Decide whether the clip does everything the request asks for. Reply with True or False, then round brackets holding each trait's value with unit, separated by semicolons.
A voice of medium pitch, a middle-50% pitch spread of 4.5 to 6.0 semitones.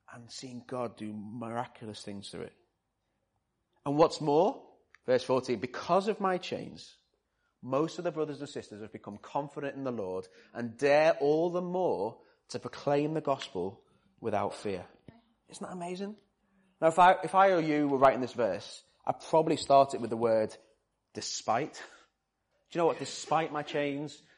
True (145 Hz; 5.5 semitones)